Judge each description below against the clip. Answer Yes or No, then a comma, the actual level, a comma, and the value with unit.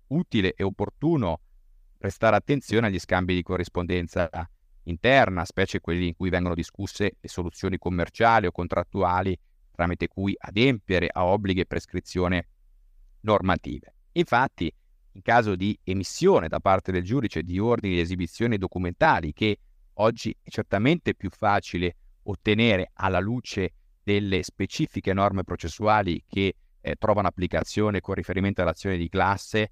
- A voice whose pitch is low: Yes, very low, 95 Hz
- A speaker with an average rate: Yes, average, 130 wpm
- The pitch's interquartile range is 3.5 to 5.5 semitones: No, average, 2.9 semitones